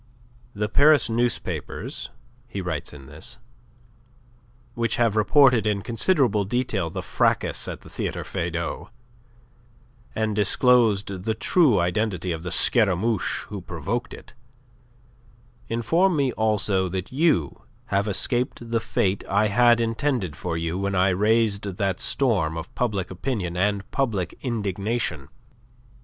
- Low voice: Yes, low, 105 Hz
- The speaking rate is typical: No, slow, 125 wpm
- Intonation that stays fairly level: No, average, 4.2 semitones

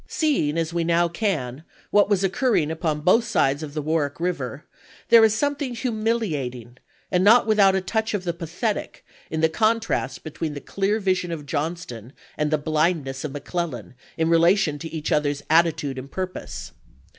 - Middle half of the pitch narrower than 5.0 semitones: No, average, 5.3 semitones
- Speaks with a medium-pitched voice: Yes, medium, 165 Hz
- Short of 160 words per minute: No, average, 175 wpm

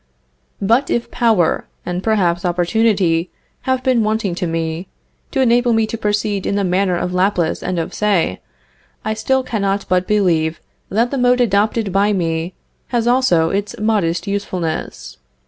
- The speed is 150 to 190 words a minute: Yes, average, 155 wpm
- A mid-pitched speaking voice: No, high, 200 Hz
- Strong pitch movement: No, average, 4.1 semitones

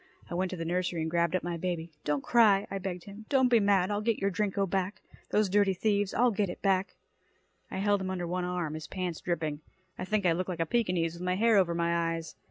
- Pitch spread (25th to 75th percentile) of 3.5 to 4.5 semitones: No, average, 2.9 semitones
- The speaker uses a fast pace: Yes, fast, 250 wpm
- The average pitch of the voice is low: No, medium, 185 Hz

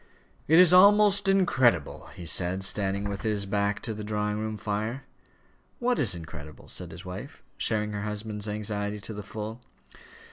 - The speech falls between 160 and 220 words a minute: Yes, average, 165 wpm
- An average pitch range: No, narrow, 2.3 semitones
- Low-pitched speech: Yes, low, 105 Hz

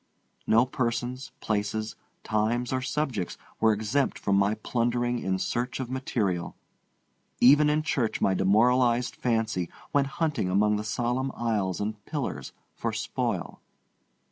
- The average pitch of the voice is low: Yes, low, 115 Hz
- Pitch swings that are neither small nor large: Yes, average, 3.3 semitones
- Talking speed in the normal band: No, slow, 130 wpm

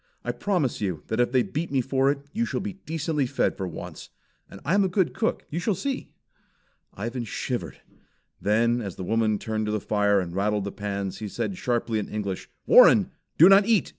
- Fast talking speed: Yes, fast, 210 wpm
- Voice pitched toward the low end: Yes, low, 120 Hz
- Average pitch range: No, wide, 8.2 semitones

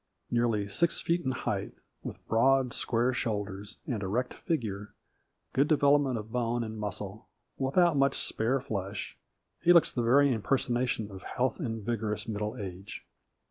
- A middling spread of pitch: Yes, average, 4.1 semitones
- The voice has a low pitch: Yes, low, 115 Hz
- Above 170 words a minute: No, average, 145 wpm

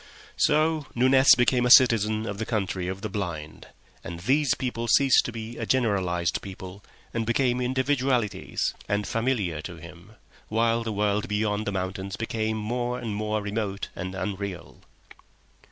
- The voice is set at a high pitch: No, low, 110 Hz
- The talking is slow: No, average, 160 wpm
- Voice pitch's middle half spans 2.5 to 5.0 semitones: Yes, average, 3.9 semitones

